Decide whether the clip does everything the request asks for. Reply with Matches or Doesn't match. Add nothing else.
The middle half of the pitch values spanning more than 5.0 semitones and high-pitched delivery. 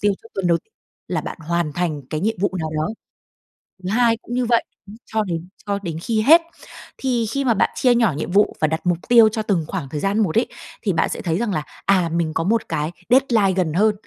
Matches